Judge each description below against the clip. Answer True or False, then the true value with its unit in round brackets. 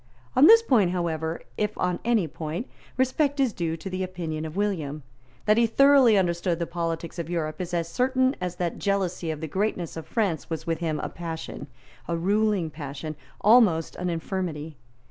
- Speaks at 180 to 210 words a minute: True (185 wpm)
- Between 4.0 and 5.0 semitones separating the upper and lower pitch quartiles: True (4.5 semitones)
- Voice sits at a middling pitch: True (175 Hz)